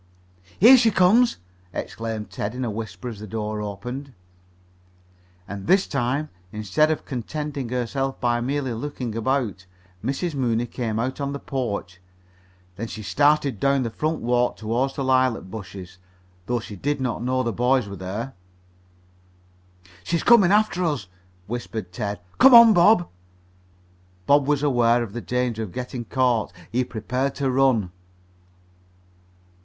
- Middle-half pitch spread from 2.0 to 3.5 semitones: No, average, 4.2 semitones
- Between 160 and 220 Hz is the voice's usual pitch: No, low, 125 Hz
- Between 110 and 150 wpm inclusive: Yes, average, 145 wpm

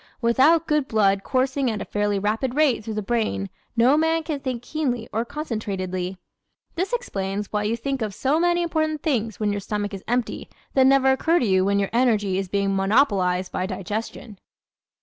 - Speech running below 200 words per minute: Yes, average, 190 wpm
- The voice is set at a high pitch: Yes, high, 230 Hz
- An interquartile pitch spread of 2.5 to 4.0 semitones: No, wide, 5.5 semitones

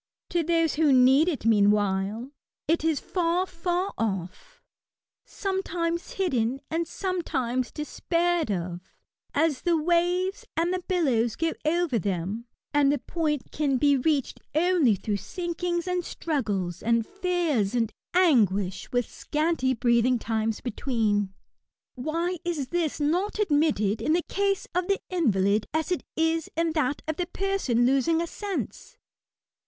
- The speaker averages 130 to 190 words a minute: Yes, average, 140 wpm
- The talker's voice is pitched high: Yes, very high, 305 Hz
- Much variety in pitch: Yes, wide, 6.9 semitones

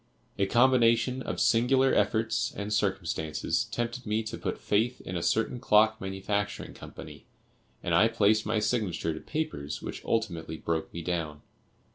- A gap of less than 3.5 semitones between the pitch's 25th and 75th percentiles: No, average, 4.6 semitones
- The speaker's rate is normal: Yes, average, 150 wpm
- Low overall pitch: Yes, low, 105 Hz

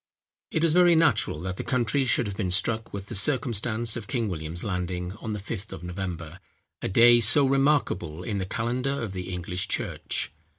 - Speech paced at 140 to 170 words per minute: No, average, 185 wpm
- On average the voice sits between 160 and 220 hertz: No, low, 105 Hz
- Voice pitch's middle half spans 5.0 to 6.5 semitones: Yes, average, 5.3 semitones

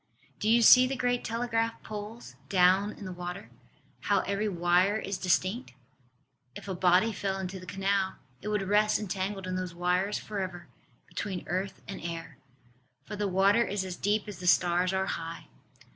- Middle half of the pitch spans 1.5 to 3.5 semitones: Yes, narrow, 2.5 semitones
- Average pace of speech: Yes, average, 175 wpm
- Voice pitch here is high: Yes, high, 195 Hz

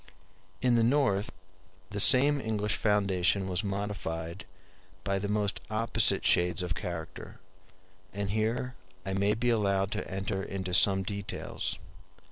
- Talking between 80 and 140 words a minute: Yes, slow, 135 wpm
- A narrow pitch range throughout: Yes, narrow, 2.1 semitones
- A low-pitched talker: Yes, low, 100 Hz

